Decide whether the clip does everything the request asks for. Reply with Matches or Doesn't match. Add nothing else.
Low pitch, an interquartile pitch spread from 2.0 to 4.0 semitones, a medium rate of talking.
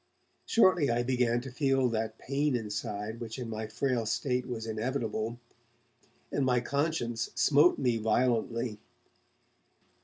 Doesn't match